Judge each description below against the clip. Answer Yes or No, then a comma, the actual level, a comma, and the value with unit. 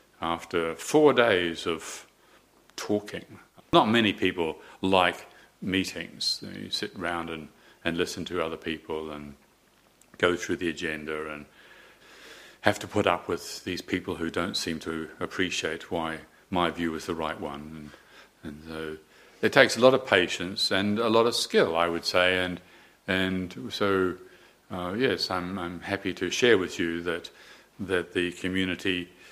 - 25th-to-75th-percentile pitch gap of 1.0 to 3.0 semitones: Yes, average, 2.7 semitones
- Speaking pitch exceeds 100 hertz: No, very low, 90 Hz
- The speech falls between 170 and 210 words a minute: No, average, 160 wpm